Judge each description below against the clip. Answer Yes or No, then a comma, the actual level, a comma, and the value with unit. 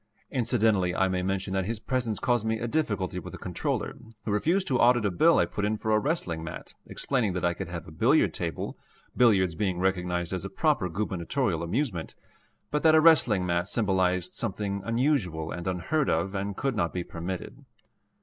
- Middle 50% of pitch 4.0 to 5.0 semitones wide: Yes, average, 4.7 semitones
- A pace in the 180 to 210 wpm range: Yes, average, 195 wpm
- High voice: No, low, 100 Hz